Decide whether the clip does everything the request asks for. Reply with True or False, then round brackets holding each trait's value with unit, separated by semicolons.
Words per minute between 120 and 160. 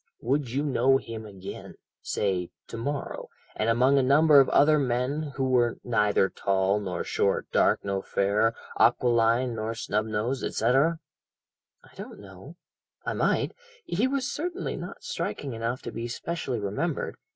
True (150 wpm)